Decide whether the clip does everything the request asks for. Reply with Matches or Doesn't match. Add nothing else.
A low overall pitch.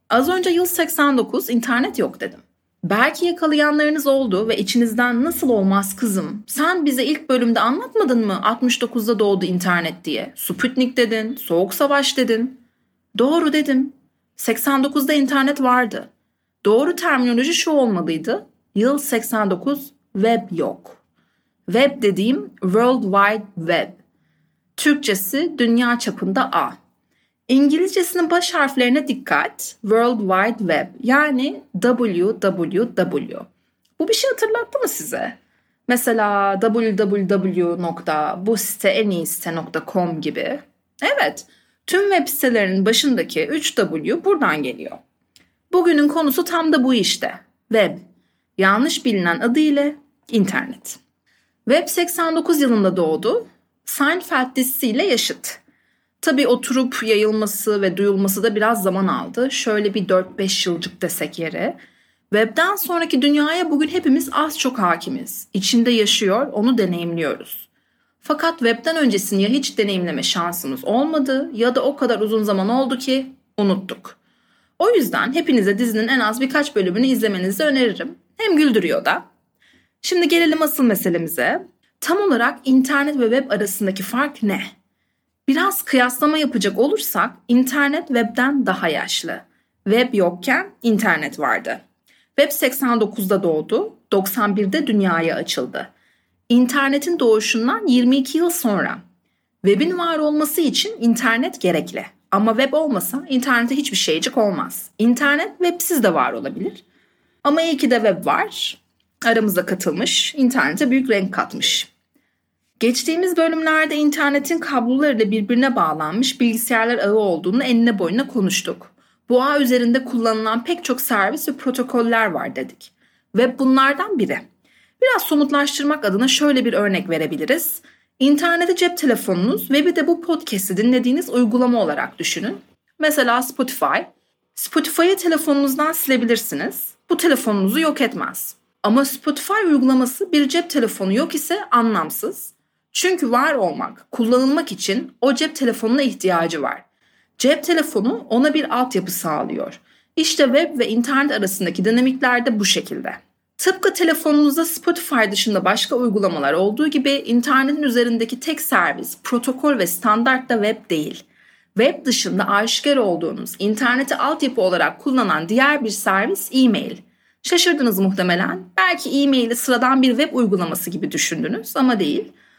Doesn't match